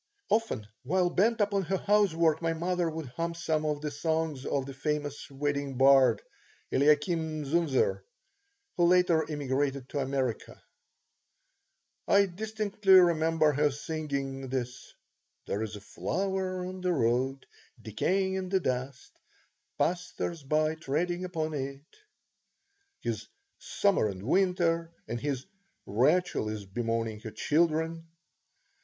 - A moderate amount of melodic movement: Yes, average, 4.8 semitones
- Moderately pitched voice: Yes, medium, 155 Hz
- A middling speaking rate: No, slow, 125 wpm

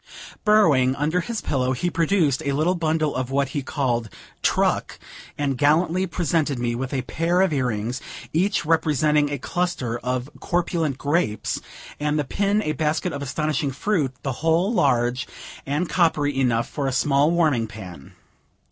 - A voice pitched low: No, medium, 145 Hz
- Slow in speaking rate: No, average, 155 wpm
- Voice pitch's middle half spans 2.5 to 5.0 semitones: Yes, average, 4.4 semitones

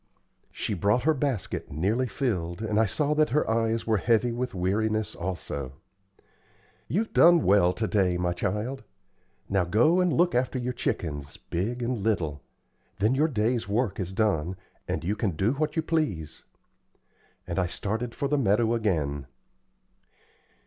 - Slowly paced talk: No, average, 155 wpm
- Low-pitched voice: Yes, low, 110 Hz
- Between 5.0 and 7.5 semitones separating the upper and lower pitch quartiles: Yes, wide, 5.6 semitones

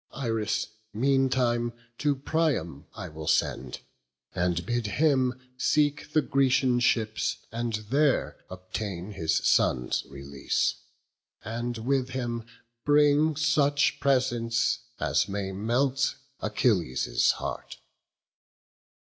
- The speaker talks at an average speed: No, slow, 100 wpm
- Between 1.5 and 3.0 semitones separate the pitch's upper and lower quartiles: No, wide, 5.5 semitones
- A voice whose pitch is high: No, low, 120 Hz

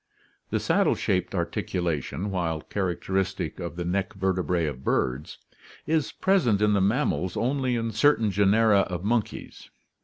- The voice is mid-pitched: No, very low, 95 Hz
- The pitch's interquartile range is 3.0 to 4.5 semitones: Yes, average, 4.0 semitones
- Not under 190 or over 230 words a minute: No, average, 145 wpm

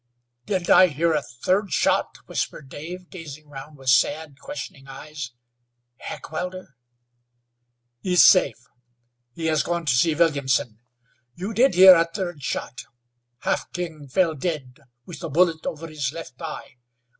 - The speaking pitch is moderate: Yes, medium, 160 Hz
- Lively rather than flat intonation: No, average, 4.0 semitones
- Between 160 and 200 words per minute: No, average, 140 wpm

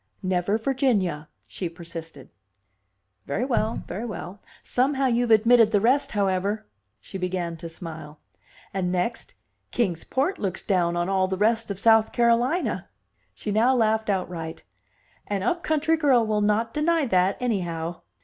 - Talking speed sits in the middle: Yes, average, 145 wpm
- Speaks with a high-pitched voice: Yes, high, 210 Hz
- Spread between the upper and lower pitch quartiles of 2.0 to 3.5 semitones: No, average, 4.8 semitones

